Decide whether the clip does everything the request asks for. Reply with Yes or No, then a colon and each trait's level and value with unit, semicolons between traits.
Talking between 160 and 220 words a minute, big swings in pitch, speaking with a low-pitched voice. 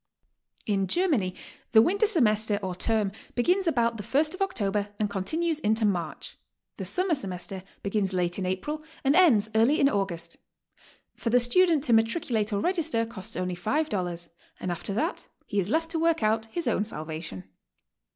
No: average, 170 wpm; wide, 8.2 semitones; high, 220 Hz